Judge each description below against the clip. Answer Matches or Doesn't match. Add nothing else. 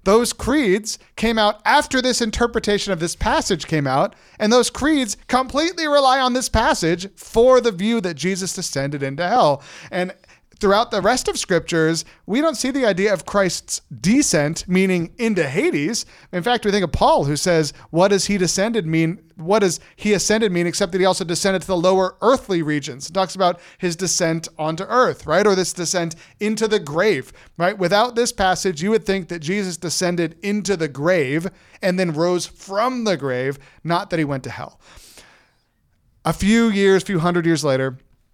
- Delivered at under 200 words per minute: Matches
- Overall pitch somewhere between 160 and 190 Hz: Matches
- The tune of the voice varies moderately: Matches